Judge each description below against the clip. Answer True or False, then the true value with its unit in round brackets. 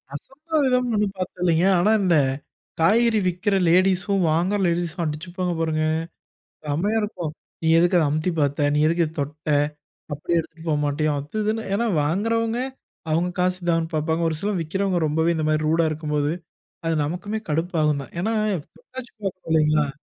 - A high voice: False (170 Hz)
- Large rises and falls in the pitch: False (4.3 semitones)